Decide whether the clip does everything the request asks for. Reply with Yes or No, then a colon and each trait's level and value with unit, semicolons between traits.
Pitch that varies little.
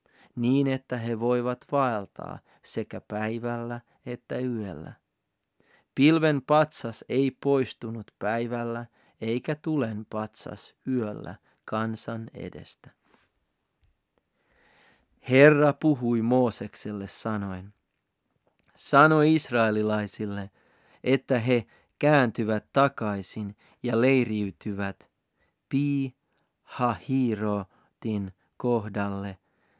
No: average, 3.8 semitones